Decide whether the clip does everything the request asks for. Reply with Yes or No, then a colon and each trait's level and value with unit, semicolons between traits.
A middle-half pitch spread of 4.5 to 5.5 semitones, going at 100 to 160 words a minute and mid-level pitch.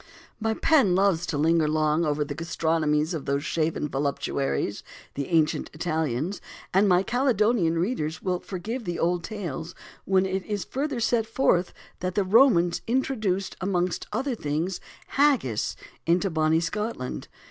Yes: average, 5.1 semitones; average, 145 wpm; medium, 175 Hz